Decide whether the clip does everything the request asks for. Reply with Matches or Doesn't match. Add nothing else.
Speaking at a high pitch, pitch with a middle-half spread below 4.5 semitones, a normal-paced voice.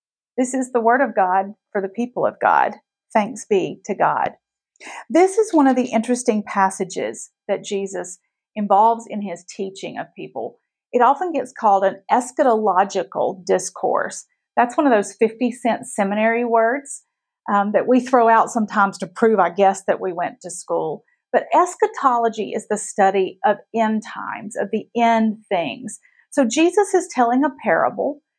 Matches